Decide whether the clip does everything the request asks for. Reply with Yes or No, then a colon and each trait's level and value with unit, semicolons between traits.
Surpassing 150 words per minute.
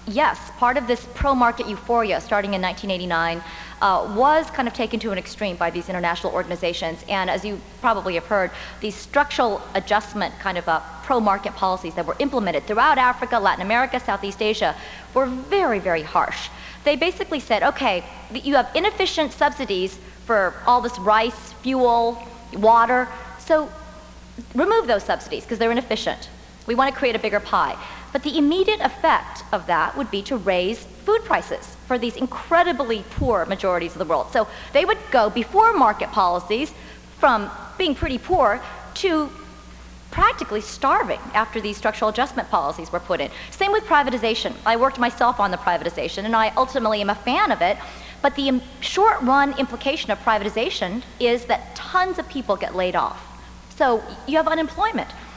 Yes: average, 165 wpm